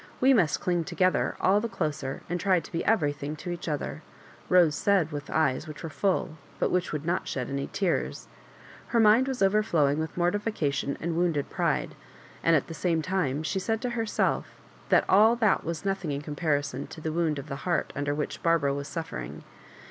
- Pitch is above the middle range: No, medium, 165 Hz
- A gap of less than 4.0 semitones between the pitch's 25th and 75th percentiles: No, average, 4.6 semitones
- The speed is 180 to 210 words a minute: Yes, average, 195 wpm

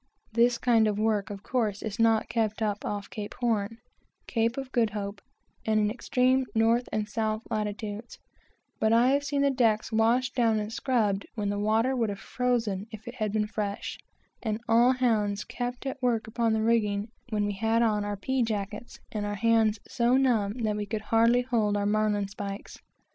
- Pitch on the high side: Yes, high, 220 Hz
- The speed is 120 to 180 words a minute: No, average, 190 wpm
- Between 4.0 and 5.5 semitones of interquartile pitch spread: No, narrow, 2.4 semitones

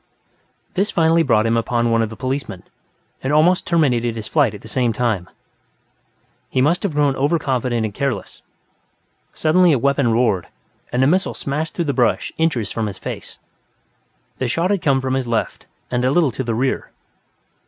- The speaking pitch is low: Yes, low, 130 Hz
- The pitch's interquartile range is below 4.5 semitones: No, average, 4.9 semitones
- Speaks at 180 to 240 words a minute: Yes, average, 185 wpm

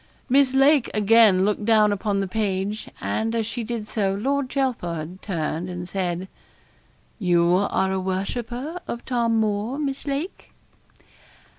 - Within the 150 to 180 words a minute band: No, average, 140 wpm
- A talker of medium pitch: No, high, 215 Hz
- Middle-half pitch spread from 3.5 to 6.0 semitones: Yes, average, 4.3 semitones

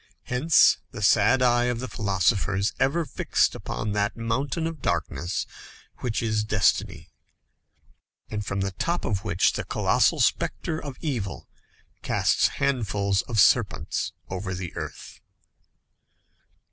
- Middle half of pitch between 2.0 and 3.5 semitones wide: No, average, 4.7 semitones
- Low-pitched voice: Yes, low, 110 Hz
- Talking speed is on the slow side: Yes, slow, 125 wpm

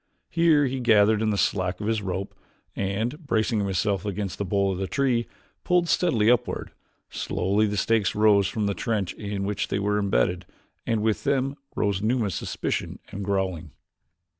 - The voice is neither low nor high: No, low, 105 Hz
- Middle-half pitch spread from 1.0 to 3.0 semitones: Yes, average, 2.7 semitones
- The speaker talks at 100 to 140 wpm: No, average, 170 wpm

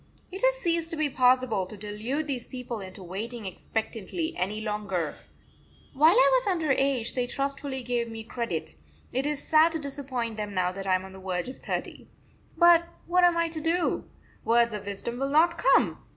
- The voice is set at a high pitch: Yes, very high, 250 Hz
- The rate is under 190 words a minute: No, average, 195 wpm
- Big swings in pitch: Yes, wide, 6.9 semitones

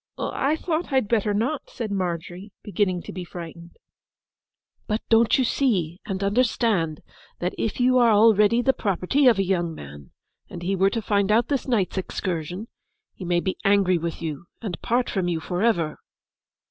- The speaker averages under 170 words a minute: No, average, 175 wpm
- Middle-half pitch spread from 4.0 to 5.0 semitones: Yes, average, 4.7 semitones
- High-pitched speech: Yes, high, 200 Hz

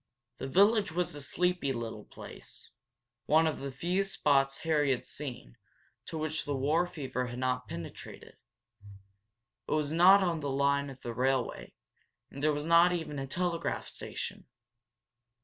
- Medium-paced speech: Yes, average, 155 wpm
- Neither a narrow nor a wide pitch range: Yes, average, 4.0 semitones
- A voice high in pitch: No, medium, 145 Hz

